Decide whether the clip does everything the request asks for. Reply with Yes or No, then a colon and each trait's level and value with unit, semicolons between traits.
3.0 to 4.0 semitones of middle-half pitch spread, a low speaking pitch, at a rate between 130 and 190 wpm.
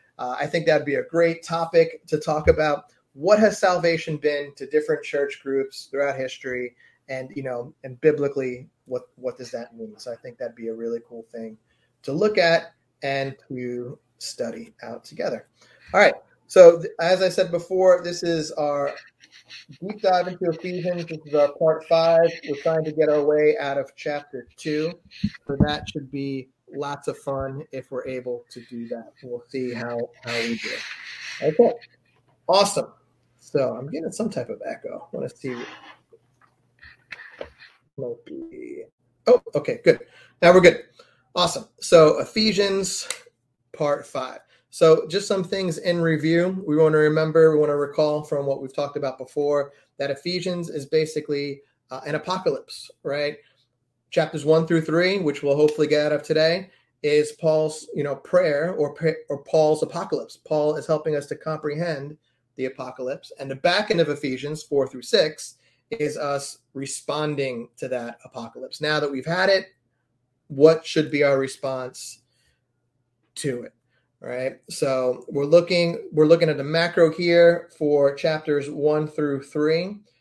No: average, 3.7 semitones; medium, 150 Hz; average, 165 wpm